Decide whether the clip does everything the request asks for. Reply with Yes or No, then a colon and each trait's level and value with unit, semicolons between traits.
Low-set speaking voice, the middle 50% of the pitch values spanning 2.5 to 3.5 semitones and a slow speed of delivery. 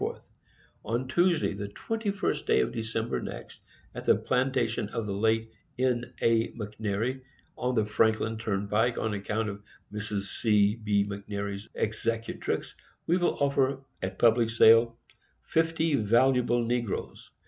Yes: low, 115 Hz; average, 3.0 semitones; slow, 130 wpm